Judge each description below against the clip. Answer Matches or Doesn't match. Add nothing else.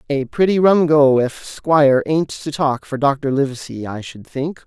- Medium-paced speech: Matches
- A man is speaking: Matches